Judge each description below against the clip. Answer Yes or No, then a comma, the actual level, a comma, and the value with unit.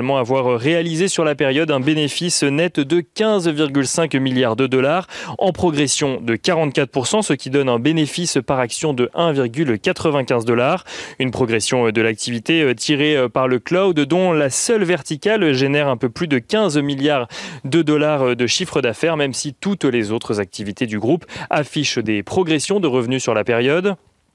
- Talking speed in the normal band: Yes, average, 165 wpm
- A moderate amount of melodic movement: Yes, average, 4.6 semitones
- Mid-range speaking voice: Yes, medium, 145 Hz